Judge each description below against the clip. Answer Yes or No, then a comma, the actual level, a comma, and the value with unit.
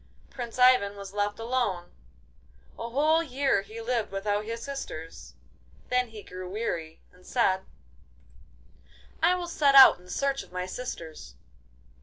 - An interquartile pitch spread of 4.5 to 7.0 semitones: Yes, wide, 5.4 semitones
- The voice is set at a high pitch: Yes, high, 225 Hz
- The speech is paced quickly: No, average, 140 wpm